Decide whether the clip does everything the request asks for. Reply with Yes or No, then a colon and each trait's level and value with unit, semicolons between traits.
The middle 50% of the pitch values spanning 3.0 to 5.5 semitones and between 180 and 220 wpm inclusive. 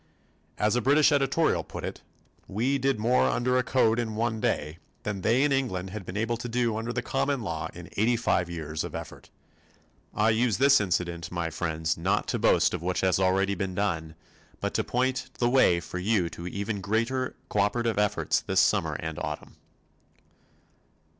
Yes: average, 5.2 semitones; average, 185 wpm